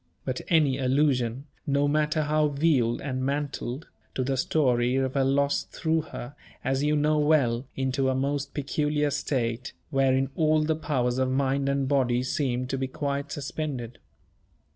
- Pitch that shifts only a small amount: Yes, narrow, 2.2 semitones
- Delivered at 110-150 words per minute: No, average, 160 wpm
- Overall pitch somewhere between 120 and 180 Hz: Yes, medium, 140 Hz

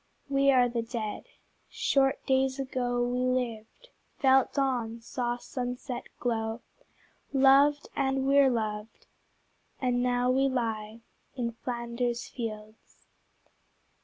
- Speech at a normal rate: No, slow, 105 wpm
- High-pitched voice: Yes, high, 245 Hz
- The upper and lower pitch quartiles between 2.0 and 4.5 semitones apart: Yes, narrow, 2.4 semitones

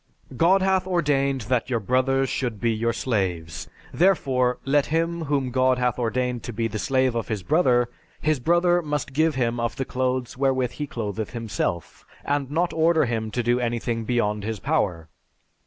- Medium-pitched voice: No, low, 125 Hz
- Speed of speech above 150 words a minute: Yes, average, 175 wpm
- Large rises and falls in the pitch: No, average, 4.0 semitones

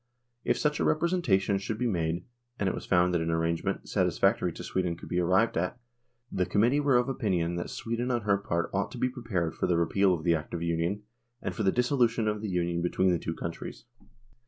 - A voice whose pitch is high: No, very low, 95 Hz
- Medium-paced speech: No, fast, 230 wpm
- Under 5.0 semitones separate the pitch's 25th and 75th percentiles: No, average, 5.3 semitones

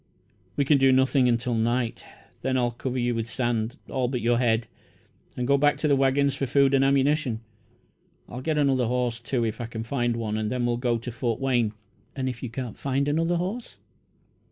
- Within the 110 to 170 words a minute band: No, fast, 205 wpm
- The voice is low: Yes, low, 125 Hz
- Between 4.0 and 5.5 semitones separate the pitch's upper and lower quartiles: No, narrow, 2.6 semitones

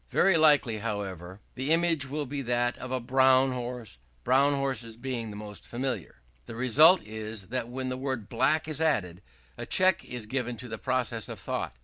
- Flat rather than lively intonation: No, average, 3.5 semitones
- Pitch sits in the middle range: No, low, 125 Hz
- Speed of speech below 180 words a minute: No, average, 190 wpm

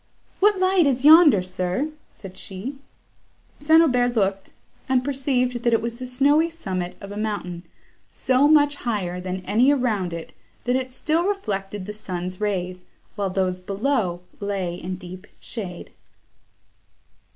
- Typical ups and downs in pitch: No, wide, 6.7 semitones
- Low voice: No, high, 215 Hz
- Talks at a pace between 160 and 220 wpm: No, average, 145 wpm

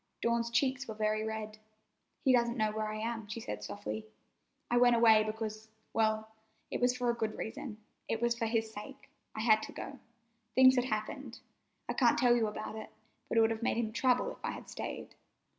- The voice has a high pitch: Yes, high, 225 Hz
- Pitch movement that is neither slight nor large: No, narrow, 1.8 semitones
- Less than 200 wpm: No, fast, 205 wpm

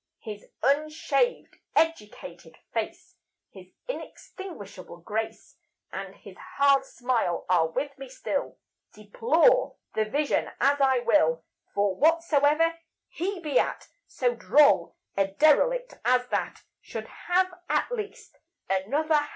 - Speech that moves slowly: Yes, slow, 120 wpm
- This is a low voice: No, very high, 280 Hz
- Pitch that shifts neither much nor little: No, wide, 7.5 semitones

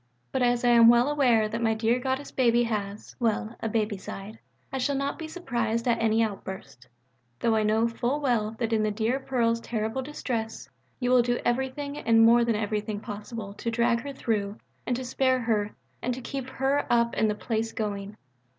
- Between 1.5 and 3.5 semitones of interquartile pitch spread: Yes, narrow, 2.5 semitones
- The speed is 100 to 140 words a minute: No, average, 200 wpm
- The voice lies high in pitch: Yes, high, 230 Hz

